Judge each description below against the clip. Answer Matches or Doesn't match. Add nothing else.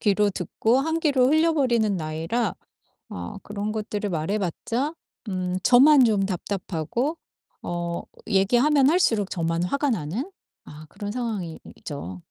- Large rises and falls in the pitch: Matches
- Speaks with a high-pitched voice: Matches